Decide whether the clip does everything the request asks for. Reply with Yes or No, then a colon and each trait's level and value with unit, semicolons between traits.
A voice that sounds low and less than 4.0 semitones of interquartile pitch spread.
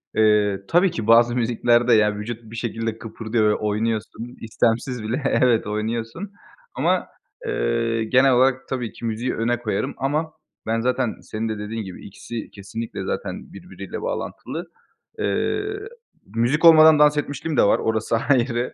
Yes: low, 115 Hz; average, 2.9 semitones